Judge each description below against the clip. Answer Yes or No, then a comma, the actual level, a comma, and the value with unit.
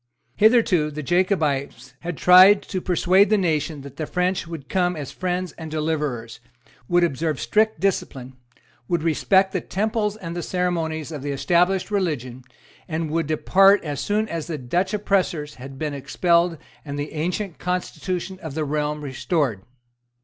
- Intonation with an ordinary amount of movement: Yes, average, 3.9 semitones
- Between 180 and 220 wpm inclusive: No, average, 155 wpm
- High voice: No, medium, 165 Hz